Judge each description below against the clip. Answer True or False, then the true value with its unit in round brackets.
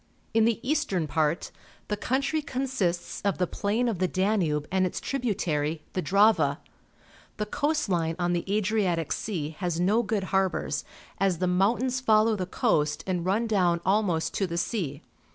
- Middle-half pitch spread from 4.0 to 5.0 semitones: True (4.3 semitones)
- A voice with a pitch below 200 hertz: True (190 Hz)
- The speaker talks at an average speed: True (165 wpm)